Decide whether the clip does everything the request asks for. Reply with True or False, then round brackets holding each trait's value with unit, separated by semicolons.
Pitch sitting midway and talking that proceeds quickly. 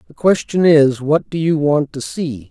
True (150 Hz; 215 wpm)